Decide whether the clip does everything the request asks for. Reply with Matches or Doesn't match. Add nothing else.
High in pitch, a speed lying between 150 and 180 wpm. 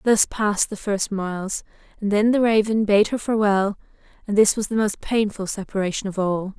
Doesn't match